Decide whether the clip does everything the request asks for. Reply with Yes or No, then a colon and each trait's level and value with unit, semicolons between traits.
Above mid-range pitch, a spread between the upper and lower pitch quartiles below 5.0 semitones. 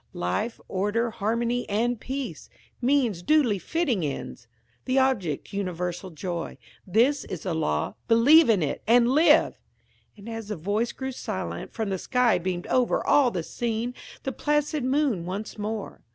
No: high, 225 Hz; wide, 5.4 semitones